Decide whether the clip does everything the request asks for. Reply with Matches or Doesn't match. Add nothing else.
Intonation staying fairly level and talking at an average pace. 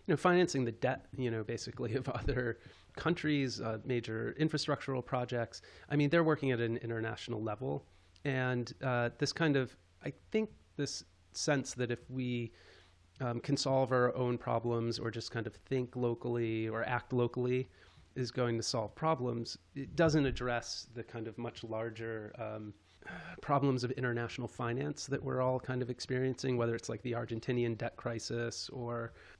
Matches